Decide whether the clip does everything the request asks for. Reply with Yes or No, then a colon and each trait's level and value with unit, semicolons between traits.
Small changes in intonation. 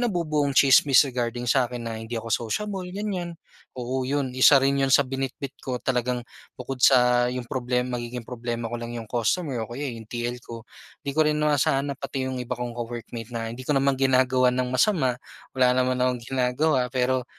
Yes: narrow, 2.1 semitones